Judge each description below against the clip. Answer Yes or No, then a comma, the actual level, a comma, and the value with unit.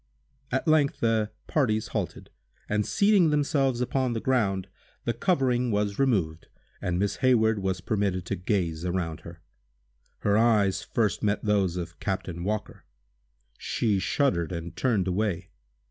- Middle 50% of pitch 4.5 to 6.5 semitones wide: Yes, average, 5.1 semitones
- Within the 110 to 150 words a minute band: Yes, average, 140 wpm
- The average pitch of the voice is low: Yes, low, 105 Hz